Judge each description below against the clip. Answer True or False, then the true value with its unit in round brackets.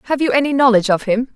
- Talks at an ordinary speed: False (265 wpm)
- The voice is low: False (245 Hz)